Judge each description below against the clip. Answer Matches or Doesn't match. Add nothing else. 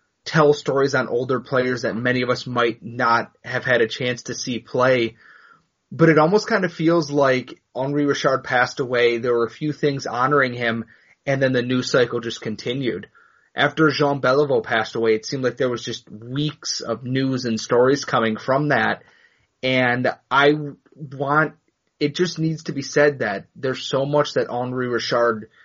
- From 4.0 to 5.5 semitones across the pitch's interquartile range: Doesn't match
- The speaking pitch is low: Matches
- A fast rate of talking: Doesn't match